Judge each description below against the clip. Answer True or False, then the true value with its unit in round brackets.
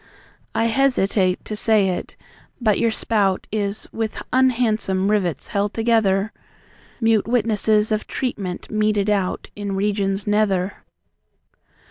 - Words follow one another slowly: True (115 wpm)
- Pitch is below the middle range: False (210 Hz)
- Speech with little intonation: True (2.2 semitones)